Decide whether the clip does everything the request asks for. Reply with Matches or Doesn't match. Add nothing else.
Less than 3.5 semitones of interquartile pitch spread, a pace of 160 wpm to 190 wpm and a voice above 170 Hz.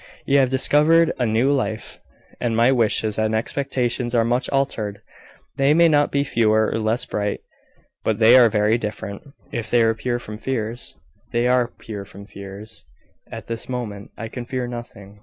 Doesn't match